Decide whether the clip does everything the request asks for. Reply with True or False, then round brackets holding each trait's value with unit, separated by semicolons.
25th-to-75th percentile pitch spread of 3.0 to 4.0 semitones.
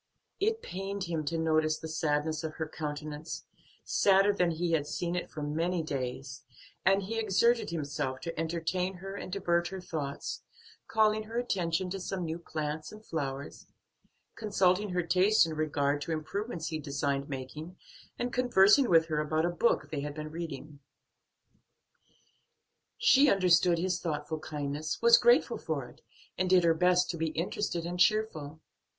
True (3.7 semitones)